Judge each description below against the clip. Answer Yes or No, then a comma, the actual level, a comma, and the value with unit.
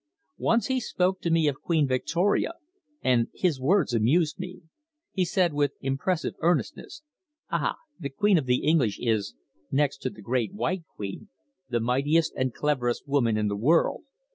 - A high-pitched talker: No, medium, 145 Hz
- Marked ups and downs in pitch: Yes, wide, 5.9 semitones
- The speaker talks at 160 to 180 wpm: Yes, average, 165 wpm